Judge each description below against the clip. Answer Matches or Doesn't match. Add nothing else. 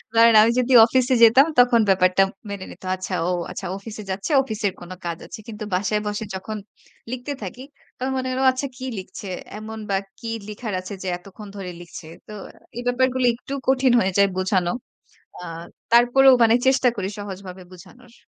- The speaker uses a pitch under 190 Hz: Doesn't match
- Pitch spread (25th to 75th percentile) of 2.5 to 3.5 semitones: Doesn't match